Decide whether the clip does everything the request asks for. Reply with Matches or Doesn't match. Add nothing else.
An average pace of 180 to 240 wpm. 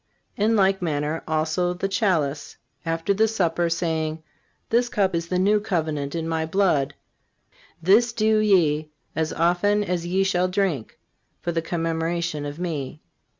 Doesn't match